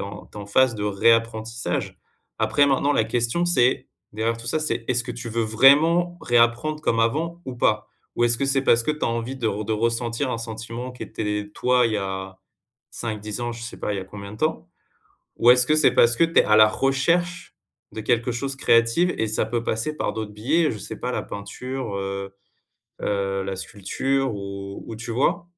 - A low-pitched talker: Yes, low, 115 Hz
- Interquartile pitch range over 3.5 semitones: Yes, average, 3.9 semitones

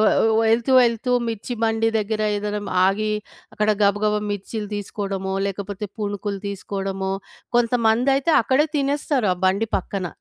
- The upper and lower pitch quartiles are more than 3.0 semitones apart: No, narrow, 2.4 semitones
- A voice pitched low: No, high, 210 Hz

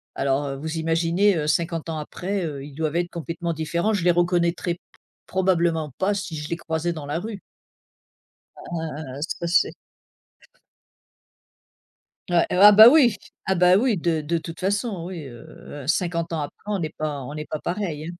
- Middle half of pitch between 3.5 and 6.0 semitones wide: No, average, 2.8 semitones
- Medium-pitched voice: Yes, medium, 170 Hz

